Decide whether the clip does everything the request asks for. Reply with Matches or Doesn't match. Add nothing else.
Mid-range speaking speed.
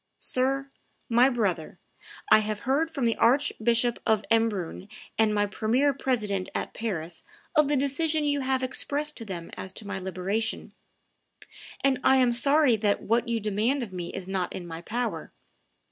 Matches